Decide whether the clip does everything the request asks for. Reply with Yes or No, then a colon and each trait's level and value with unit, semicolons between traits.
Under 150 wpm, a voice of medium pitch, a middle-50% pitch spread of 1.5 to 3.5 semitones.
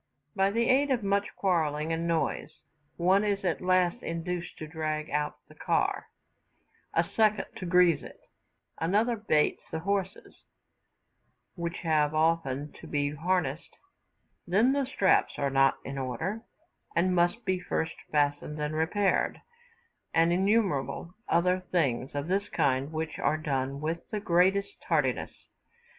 No: average, 140 wpm; medium, 170 Hz; average, 4.2 semitones